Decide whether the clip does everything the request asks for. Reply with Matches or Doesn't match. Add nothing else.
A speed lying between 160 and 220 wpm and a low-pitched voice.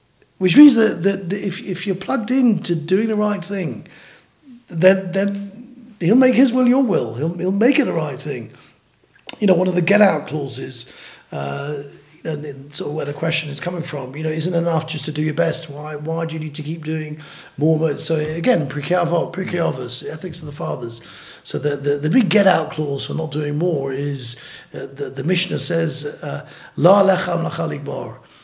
Doesn't match